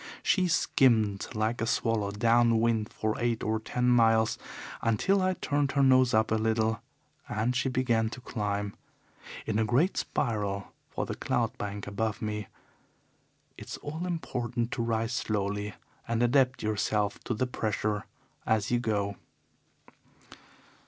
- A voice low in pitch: Yes, low, 115 Hz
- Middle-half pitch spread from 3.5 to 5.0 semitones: No, narrow, 2.6 semitones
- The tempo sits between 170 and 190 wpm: No, average, 145 wpm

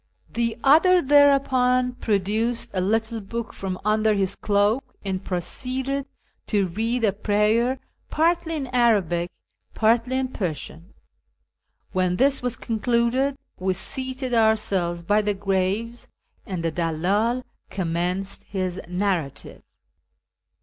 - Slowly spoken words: Yes, slow, 115 wpm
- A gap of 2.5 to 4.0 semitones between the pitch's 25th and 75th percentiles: No, average, 4.9 semitones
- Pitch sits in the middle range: No, high, 220 Hz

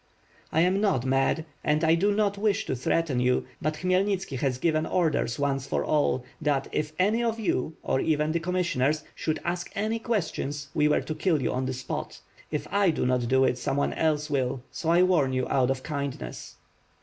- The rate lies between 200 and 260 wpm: Yes, fast, 205 wpm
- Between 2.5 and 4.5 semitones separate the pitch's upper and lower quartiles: No, average, 5.3 semitones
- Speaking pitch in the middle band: Yes, medium, 155 Hz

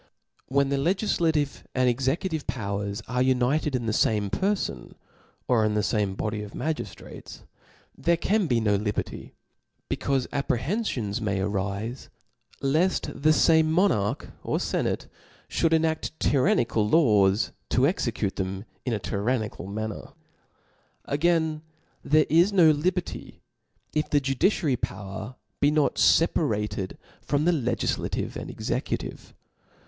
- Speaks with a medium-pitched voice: No, low, 130 Hz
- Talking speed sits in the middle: No, slow, 125 wpm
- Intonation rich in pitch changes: Yes, wide, 7.0 semitones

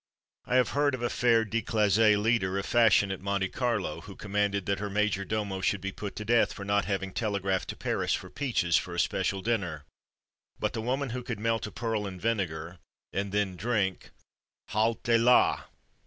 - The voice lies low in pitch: Yes, low, 105 Hz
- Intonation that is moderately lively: Yes, average, 3.0 semitones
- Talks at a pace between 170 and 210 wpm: Yes, average, 190 wpm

